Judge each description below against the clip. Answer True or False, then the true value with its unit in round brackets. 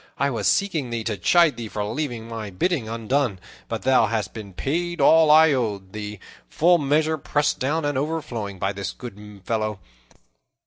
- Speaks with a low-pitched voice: True (120 Hz)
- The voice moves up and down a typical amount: False (6.2 semitones)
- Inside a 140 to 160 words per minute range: False (175 wpm)